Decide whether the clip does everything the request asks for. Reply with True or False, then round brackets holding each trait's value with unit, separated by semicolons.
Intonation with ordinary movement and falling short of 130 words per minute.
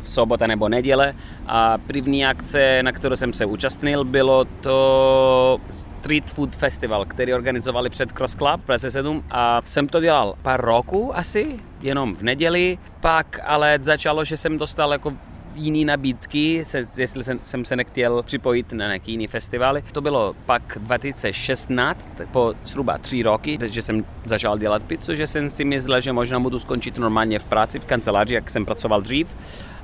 False (3.5 semitones; 170 wpm)